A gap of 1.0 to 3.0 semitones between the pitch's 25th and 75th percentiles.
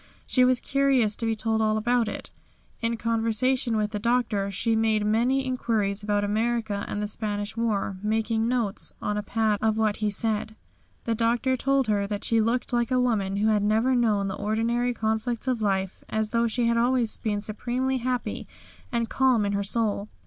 Yes: narrow, 2.4 semitones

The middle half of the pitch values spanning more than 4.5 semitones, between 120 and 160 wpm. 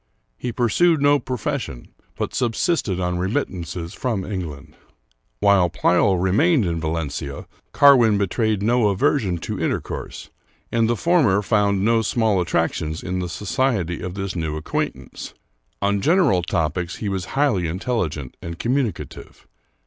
Yes: wide, 5.4 semitones; average, 140 wpm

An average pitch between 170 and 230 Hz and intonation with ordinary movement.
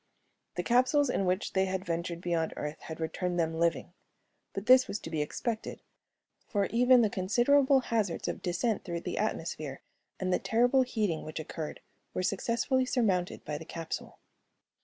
No: high, 190 Hz; wide, 6.2 semitones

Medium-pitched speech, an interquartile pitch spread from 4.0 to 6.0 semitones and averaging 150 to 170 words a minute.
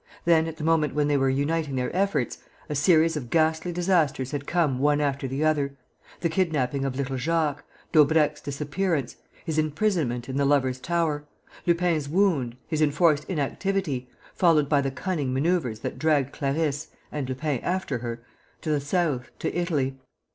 No: medium, 150 Hz; average, 3.3 semitones; average, 165 wpm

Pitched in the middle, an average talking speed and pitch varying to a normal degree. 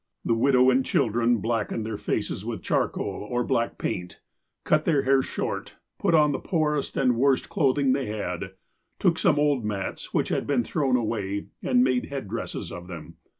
No: low, 125 Hz; average, 180 wpm; average, 4.2 semitones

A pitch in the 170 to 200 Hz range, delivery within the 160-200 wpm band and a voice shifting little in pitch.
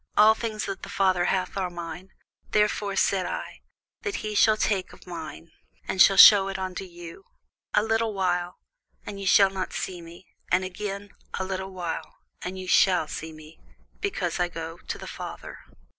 Yes: high, 190 Hz; average, 180 wpm; narrow, 2.2 semitones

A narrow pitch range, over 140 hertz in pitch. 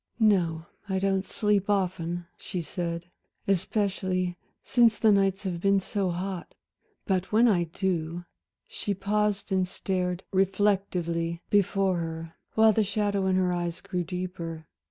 Yes: narrow, 2.3 semitones; high, 190 Hz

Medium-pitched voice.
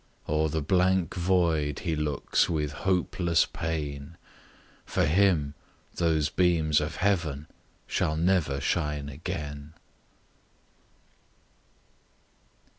No: very low, 80 Hz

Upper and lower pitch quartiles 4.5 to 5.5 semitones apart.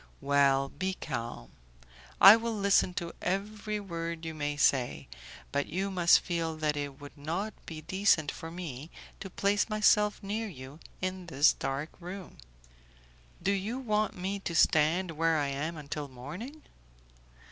Yes: average, 5.2 semitones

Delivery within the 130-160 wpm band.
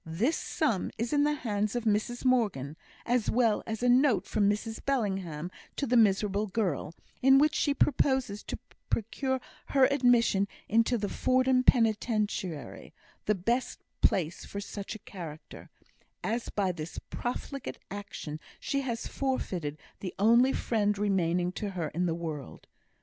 Yes: average, 150 wpm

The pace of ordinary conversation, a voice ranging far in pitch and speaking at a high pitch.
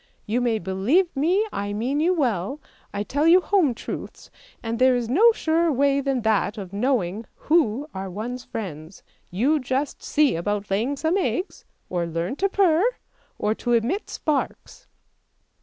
Yes: average, 160 wpm; wide, 6.9 semitones; very high, 250 Hz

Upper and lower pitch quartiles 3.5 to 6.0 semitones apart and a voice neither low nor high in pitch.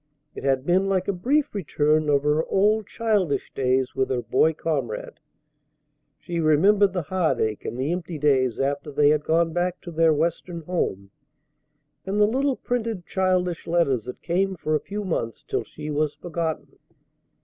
Yes: average, 4.5 semitones; medium, 165 Hz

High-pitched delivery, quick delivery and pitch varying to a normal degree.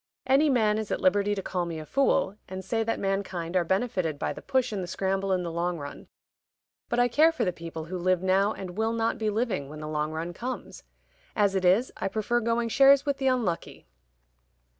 Yes: high, 195 Hz; fast, 225 wpm; average, 4.6 semitones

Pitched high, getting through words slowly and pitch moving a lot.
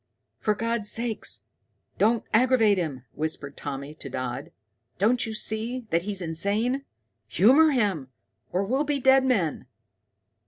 Yes: high, 210 Hz; slow, 130 wpm; wide, 7.3 semitones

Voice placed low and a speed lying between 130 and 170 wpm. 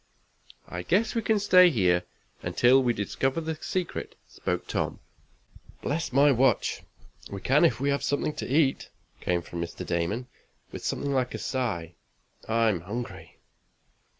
Yes: low, 130 Hz; average, 150 wpm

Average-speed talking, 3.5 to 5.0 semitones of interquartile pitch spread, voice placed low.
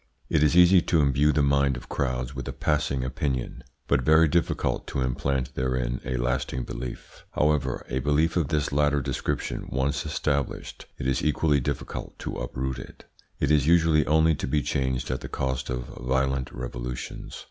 No: average, 175 wpm; average, 2.7 semitones; very low, 70 Hz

